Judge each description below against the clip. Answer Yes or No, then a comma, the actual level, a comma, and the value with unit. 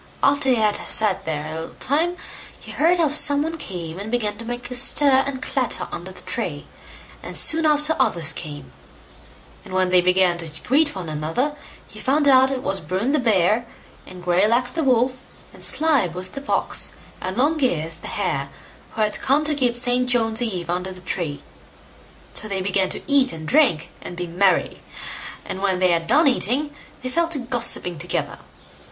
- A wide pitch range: Yes, wide, 7.3 semitones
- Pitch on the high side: Yes, high, 230 Hz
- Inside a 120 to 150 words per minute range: No, average, 185 wpm